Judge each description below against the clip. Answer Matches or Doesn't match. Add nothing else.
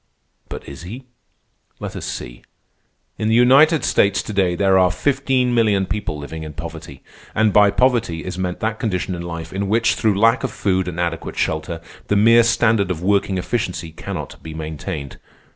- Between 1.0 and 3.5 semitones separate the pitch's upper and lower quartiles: Doesn't match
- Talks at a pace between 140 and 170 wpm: Doesn't match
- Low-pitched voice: Matches